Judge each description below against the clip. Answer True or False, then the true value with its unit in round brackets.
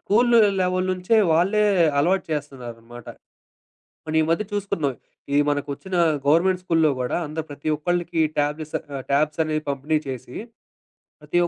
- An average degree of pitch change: True (4.1 semitones)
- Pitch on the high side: False (155 Hz)